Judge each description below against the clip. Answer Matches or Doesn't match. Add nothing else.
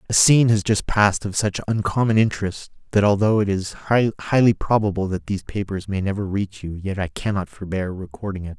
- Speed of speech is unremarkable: Matches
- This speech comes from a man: Matches